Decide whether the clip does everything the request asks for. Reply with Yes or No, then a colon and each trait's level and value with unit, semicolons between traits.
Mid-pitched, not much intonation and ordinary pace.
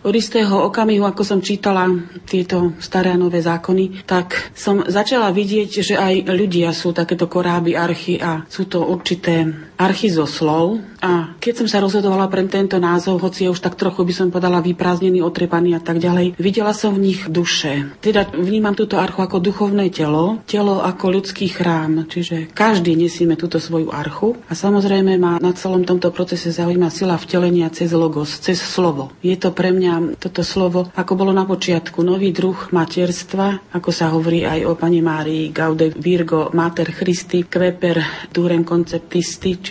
No: medium, 180 Hz; narrow, 2.2 semitones; fast, 170 wpm